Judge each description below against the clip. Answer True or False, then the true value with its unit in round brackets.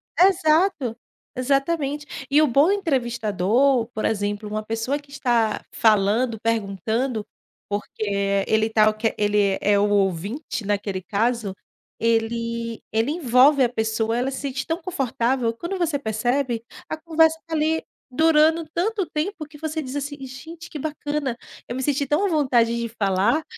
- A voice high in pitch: True (250 Hz)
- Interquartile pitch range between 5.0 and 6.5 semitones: True (5.5 semitones)